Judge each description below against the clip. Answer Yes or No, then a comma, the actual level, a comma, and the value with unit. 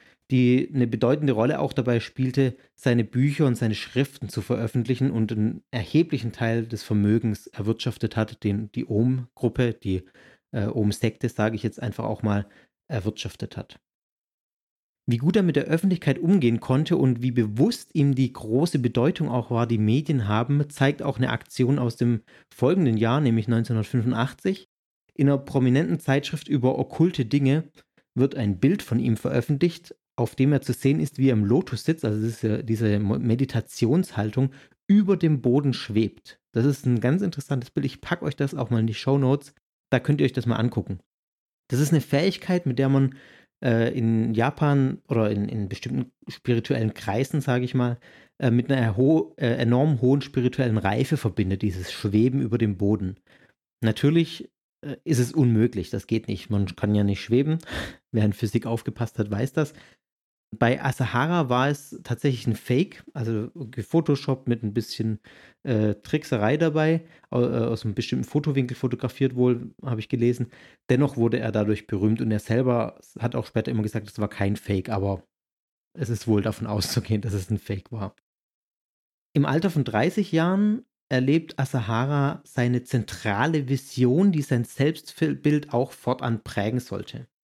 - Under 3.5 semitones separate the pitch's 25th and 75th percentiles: No, average, 3.8 semitones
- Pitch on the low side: Yes, low, 125 Hz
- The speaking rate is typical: Yes, average, 170 wpm